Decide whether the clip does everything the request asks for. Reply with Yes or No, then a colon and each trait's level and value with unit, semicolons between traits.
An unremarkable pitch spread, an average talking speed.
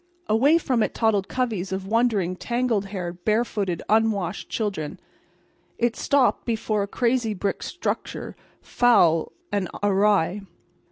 No: average, 3.6 semitones; slow, 120 wpm